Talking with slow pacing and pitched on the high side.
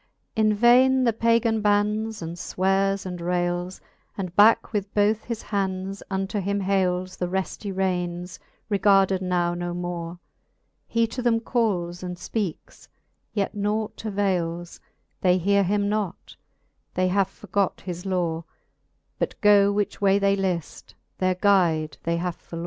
No: average, 145 wpm; high, 195 Hz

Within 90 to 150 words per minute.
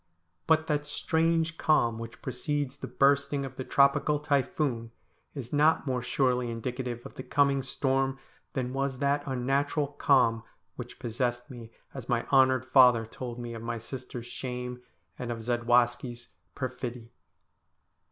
Yes: average, 140 wpm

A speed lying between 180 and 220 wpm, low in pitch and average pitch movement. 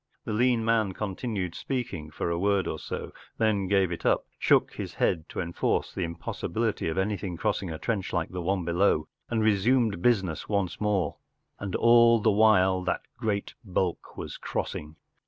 Yes: average, 185 wpm; low, 100 Hz; average, 3.8 semitones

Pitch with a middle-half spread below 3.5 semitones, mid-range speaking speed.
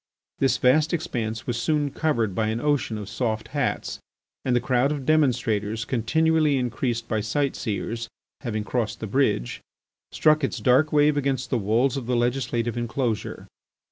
No: average, 3.9 semitones; average, 160 wpm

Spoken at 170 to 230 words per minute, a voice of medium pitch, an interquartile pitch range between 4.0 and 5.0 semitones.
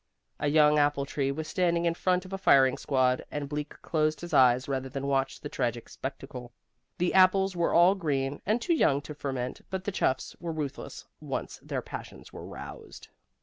Yes: average, 190 wpm; medium, 145 Hz; average, 4.3 semitones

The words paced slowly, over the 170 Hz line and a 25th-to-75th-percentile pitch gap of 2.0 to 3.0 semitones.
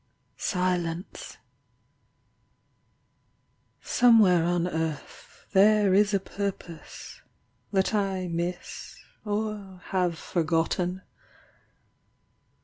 Yes: slow, 65 wpm; medium, 185 Hz; narrow, 2.6 semitones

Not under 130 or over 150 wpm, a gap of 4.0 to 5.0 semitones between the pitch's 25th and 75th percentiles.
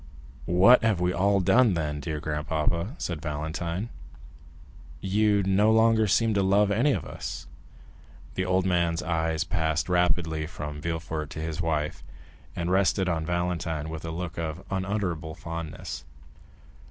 No: average, 140 wpm; average, 3.3 semitones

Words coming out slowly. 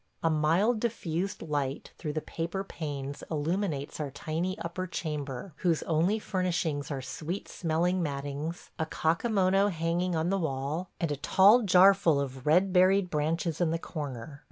No: average, 155 wpm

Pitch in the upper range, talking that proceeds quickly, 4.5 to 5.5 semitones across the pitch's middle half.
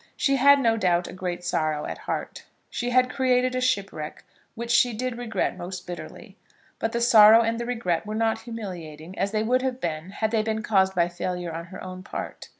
Yes: high, 215 Hz; fast, 210 wpm; average, 5.0 semitones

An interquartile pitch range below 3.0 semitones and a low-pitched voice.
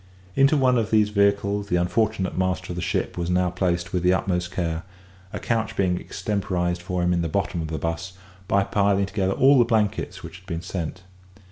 Yes: narrow, 2.5 semitones; very low, 95 Hz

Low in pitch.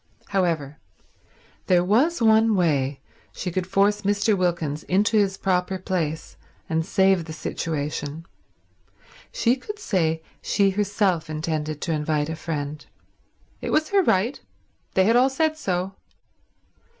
No: medium, 185 Hz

